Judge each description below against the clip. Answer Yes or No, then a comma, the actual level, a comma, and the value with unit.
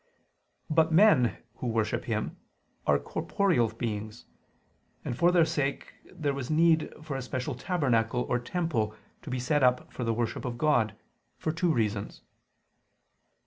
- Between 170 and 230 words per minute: No, average, 145 wpm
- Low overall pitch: Yes, low, 130 Hz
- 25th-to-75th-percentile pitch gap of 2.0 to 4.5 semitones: No, wide, 5.5 semitones